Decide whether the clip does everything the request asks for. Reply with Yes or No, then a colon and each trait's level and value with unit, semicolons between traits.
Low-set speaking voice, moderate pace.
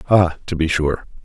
Yes: very low, 85 Hz; average, 195 wpm